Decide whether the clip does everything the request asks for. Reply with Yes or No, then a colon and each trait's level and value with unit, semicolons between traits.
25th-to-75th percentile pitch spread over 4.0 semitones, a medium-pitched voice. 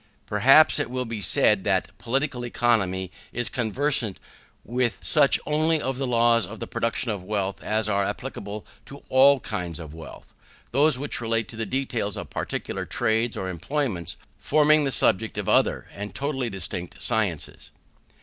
No: average, 4.9 semitones; low, 115 Hz